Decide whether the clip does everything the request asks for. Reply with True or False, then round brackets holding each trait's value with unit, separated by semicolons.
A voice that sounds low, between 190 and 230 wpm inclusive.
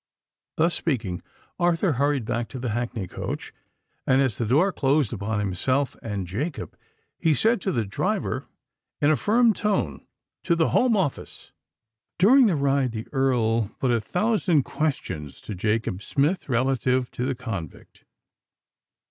False (130 Hz; 150 wpm)